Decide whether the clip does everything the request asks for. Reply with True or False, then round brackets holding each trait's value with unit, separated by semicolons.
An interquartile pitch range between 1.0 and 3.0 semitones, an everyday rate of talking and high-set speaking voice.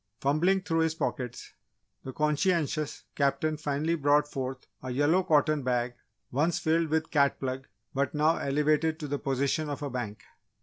False (2.6 semitones; 160 wpm; 150 Hz)